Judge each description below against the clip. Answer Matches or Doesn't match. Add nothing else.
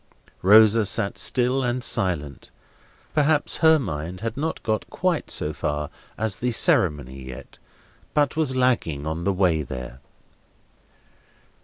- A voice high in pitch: Doesn't match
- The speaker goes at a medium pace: Doesn't match